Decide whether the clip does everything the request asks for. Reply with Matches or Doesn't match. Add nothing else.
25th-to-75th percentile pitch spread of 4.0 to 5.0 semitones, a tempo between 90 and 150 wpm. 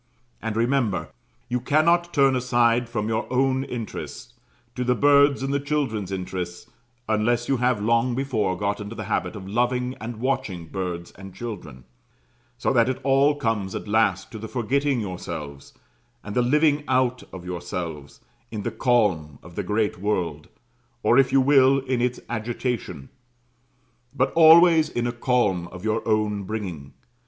Doesn't match